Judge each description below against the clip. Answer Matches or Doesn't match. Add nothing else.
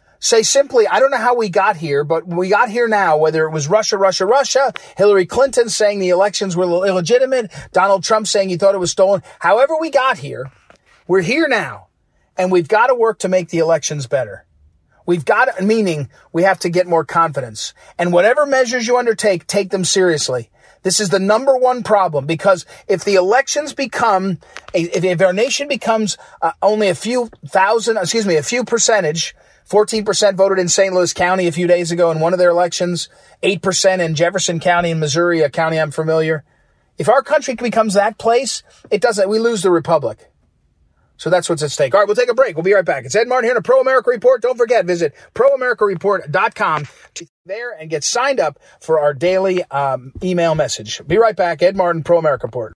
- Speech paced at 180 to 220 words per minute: Matches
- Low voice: Doesn't match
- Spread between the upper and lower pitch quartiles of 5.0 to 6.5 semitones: Matches